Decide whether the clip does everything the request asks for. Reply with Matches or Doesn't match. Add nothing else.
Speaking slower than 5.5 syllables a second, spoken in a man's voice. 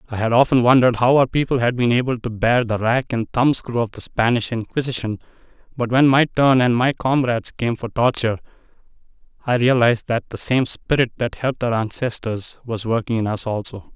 Doesn't match